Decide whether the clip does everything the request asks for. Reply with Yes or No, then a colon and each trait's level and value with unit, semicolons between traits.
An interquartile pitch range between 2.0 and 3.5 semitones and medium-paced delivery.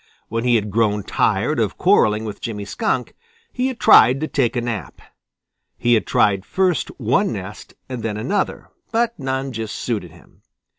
No: average, 4.4 semitones; average, 170 wpm